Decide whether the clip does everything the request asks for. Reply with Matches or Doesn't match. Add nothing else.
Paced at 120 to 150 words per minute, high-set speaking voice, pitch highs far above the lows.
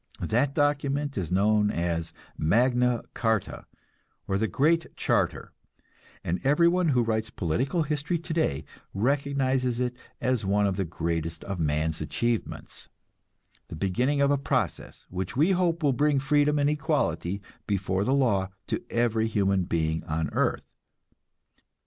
Doesn't match